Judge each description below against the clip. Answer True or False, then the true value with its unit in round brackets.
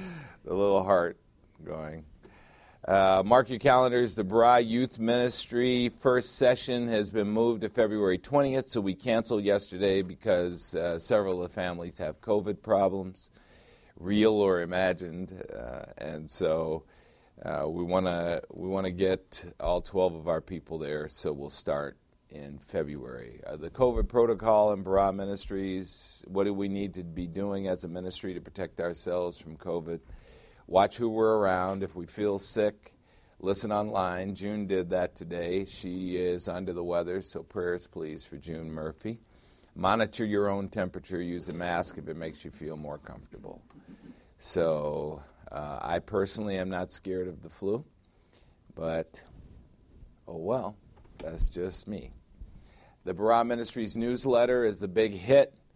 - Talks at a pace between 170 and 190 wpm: False (150 wpm)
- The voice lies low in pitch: True (95 Hz)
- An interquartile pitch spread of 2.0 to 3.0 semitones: False (3.8 semitones)